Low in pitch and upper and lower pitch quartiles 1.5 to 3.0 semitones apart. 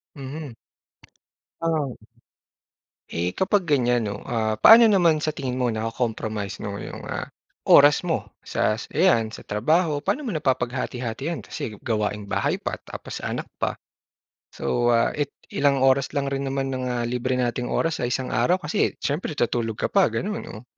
No: low, 130 Hz; average, 4.6 semitones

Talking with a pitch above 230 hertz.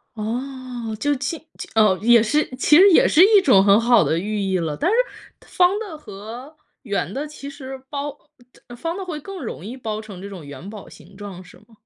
Yes: high, 240 Hz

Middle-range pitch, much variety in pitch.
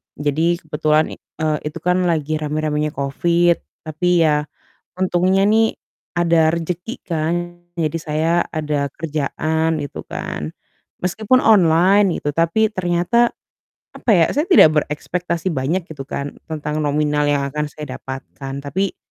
No: medium, 160 Hz; average, 3.0 semitones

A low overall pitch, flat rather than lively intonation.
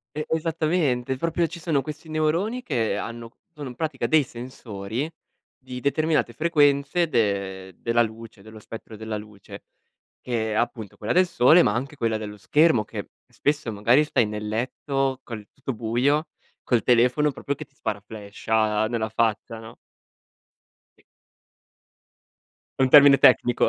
No: low, 120 Hz; average, 5.2 semitones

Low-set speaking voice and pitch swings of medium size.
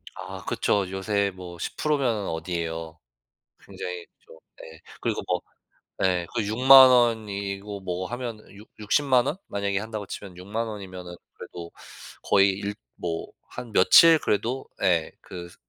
Yes: low, 100 Hz; average, 4.0 semitones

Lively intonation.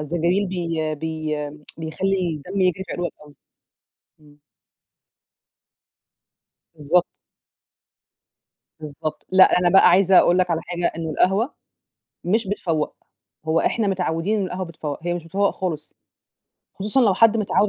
No: average, 3.4 semitones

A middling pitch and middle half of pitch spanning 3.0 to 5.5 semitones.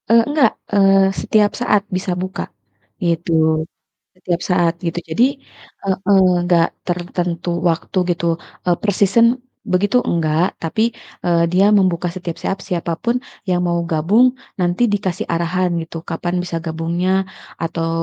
No: medium, 180 Hz; narrow, 2.4 semitones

